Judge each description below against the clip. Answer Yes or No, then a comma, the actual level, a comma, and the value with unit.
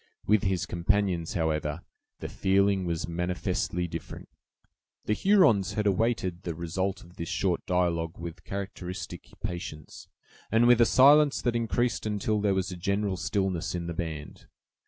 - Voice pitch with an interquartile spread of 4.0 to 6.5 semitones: No, average, 3.4 semitones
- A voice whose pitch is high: No, very low, 95 Hz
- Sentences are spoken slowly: No, average, 150 wpm